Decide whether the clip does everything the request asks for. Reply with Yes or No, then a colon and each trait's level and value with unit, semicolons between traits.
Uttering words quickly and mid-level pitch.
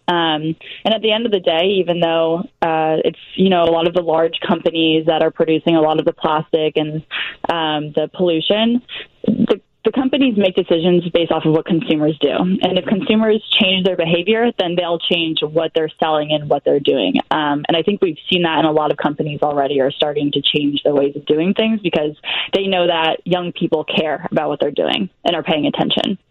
Yes: fast, 220 wpm; medium, 165 Hz